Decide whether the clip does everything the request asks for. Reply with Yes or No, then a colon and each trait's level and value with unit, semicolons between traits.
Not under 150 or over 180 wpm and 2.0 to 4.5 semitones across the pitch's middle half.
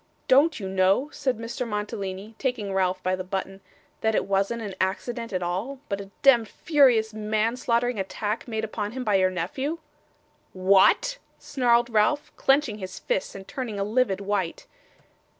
Yes: average, 160 wpm; average, 4.2 semitones